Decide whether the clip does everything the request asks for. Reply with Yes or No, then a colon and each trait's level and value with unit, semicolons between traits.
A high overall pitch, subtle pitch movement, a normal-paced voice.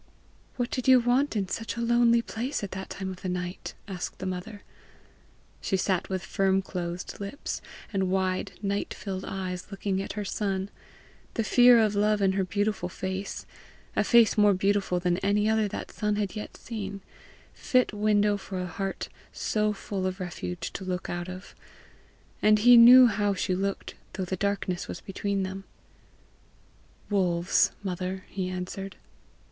Yes: high, 195 Hz; narrow, 2.2 semitones; average, 165 wpm